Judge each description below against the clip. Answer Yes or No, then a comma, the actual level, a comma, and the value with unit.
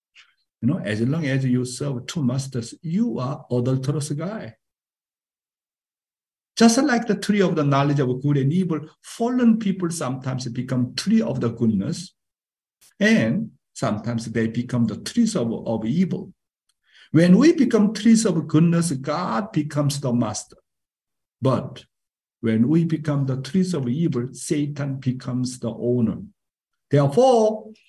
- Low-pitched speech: No, medium, 150 Hz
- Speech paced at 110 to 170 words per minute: Yes, average, 140 wpm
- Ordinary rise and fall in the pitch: No, wide, 7.2 semitones